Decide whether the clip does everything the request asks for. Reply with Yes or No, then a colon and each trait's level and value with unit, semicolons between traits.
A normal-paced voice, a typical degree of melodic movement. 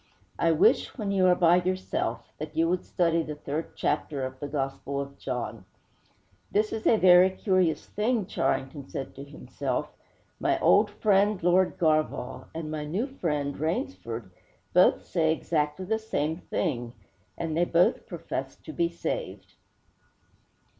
Yes: average, 150 wpm; average, 4.2 semitones